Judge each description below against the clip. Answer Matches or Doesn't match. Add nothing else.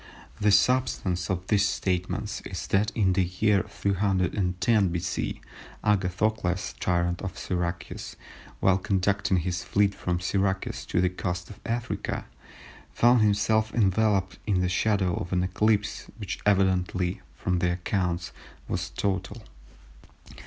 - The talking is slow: Matches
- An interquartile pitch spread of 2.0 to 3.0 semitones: Matches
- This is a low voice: Matches